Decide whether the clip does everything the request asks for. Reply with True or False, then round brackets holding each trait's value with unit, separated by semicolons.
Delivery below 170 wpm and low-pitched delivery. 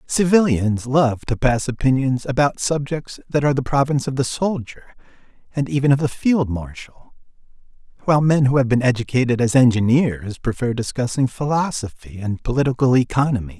True (150 wpm; 130 Hz)